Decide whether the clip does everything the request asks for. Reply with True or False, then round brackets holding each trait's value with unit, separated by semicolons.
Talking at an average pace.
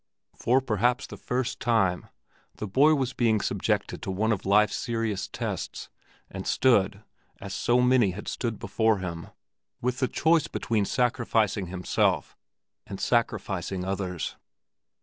False (130 wpm)